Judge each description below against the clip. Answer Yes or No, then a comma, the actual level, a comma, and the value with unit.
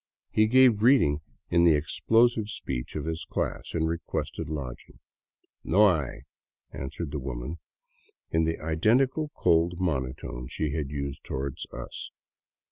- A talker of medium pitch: No, very low, 80 Hz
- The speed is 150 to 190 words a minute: No, slow, 135 wpm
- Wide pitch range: Yes, wide, 6.6 semitones